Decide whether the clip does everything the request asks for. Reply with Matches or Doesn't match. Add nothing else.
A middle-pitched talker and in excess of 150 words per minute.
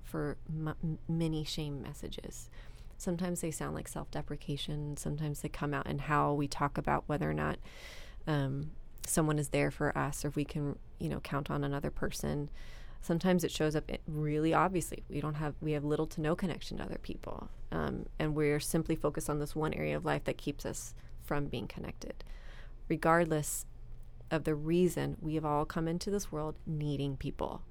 Matches